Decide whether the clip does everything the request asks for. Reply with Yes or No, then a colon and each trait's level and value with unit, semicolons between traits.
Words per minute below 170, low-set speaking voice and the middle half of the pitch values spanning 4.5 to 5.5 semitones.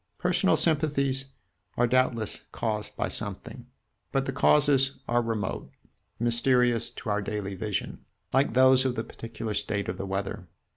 No: average, 145 wpm; low, 120 Hz; average, 4.1 semitones